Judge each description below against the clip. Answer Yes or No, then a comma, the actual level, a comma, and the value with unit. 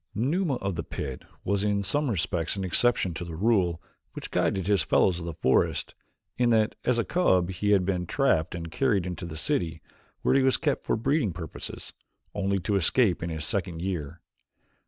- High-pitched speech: No, very low, 95 Hz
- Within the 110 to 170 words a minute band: No, average, 195 wpm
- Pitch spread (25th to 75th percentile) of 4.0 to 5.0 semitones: Yes, average, 4.7 semitones